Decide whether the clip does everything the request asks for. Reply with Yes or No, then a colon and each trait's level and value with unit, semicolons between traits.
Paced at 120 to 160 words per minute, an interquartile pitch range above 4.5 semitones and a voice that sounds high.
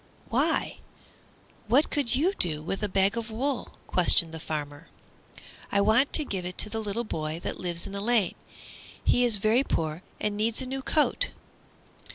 No: average, 180 wpm; wide, 5.5 semitones; high, 210 Hz